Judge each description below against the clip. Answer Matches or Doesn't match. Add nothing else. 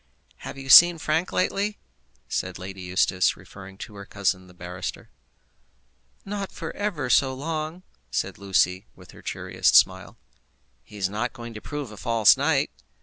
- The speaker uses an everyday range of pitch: Doesn't match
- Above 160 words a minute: Doesn't match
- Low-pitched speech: Matches